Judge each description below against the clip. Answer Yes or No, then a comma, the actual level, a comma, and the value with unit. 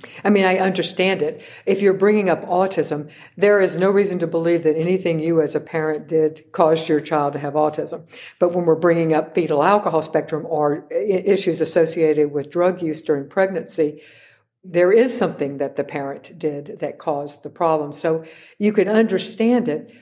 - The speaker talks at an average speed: Yes, average, 185 wpm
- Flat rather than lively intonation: No, average, 3.6 semitones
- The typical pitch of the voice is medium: Yes, medium, 165 Hz